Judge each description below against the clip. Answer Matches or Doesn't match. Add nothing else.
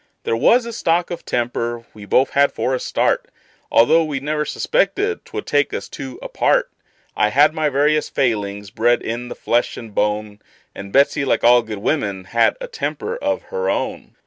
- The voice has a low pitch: Matches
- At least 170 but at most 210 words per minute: Matches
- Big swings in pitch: Matches